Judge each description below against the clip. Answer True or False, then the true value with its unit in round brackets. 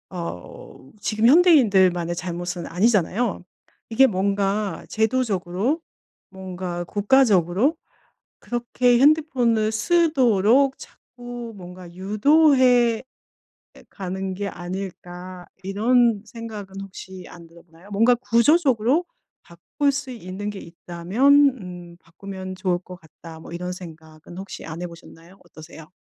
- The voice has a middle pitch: False (195 Hz)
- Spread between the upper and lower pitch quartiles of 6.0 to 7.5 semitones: False (5.3 semitones)